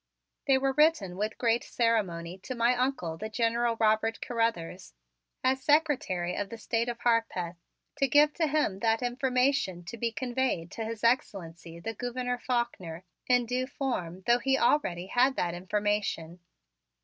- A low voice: No, high, 230 Hz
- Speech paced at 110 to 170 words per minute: Yes, average, 155 wpm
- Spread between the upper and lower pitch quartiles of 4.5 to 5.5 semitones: Yes, average, 5.1 semitones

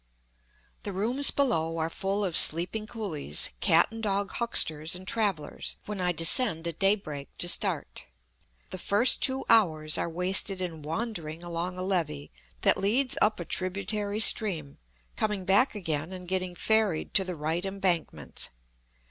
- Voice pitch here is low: No, medium, 185 Hz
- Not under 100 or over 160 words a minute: Yes, average, 155 wpm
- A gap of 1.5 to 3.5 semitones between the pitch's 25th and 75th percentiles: No, average, 4.2 semitones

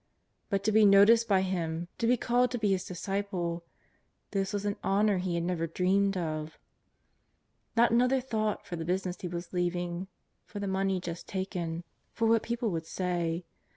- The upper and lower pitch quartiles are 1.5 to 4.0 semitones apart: Yes, average, 3.2 semitones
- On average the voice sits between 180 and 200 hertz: Yes, high, 190 Hz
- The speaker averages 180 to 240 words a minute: Yes, average, 185 wpm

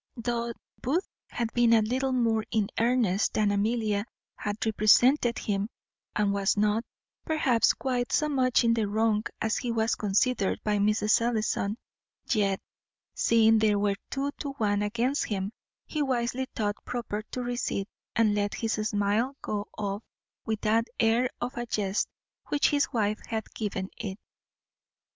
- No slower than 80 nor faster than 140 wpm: No, average, 155 wpm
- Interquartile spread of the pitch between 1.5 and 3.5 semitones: Yes, average, 2.7 semitones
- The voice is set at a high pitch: Yes, high, 220 Hz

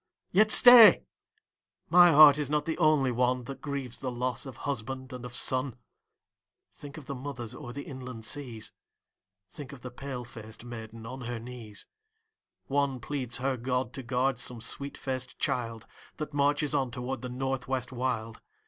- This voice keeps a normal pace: Yes, average, 170 wpm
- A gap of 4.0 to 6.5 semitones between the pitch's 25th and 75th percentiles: No, narrow, 2.6 semitones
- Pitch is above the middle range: No, low, 130 Hz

